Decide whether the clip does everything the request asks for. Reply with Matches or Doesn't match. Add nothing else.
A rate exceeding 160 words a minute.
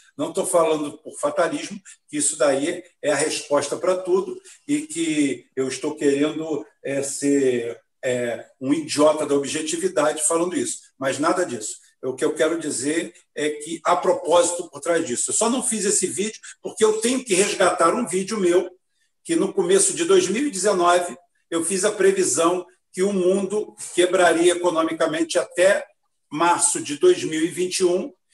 Doesn't match